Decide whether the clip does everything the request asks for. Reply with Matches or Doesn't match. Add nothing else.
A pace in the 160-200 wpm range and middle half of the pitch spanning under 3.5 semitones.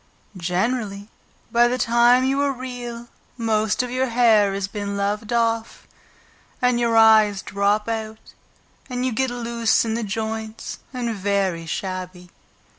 Doesn't match